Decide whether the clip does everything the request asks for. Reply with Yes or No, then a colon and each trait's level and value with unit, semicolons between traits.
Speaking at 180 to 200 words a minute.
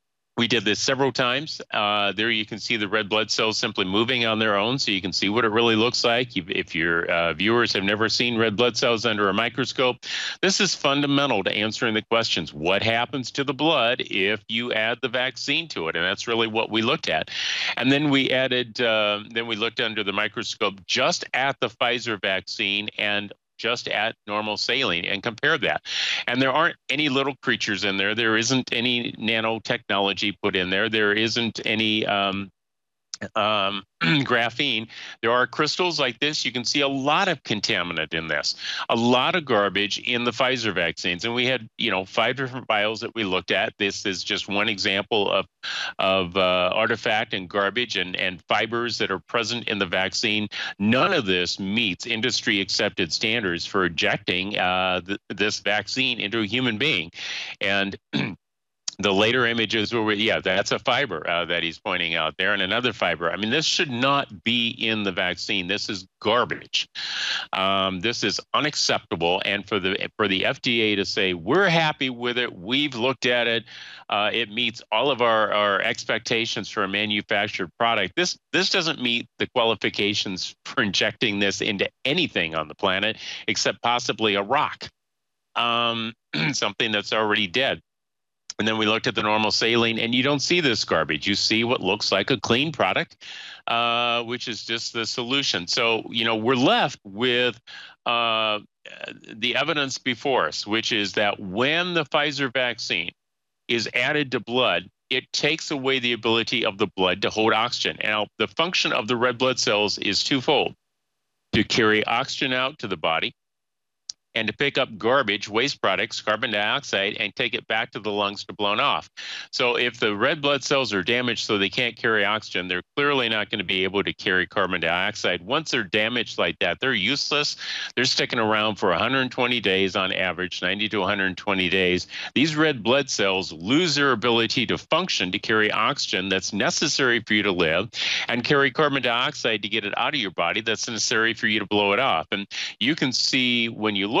Yes: average, 190 wpm